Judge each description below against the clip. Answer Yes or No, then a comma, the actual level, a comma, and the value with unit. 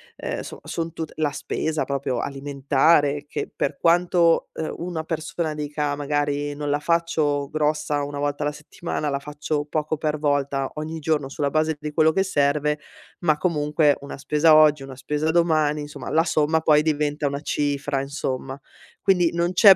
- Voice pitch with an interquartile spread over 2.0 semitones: No, narrow, 1.7 semitones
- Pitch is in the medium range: Yes, medium, 150 Hz